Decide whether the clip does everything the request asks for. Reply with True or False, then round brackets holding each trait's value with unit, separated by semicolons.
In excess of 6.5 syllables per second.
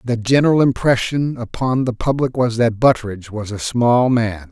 False (5.1 syllables/s)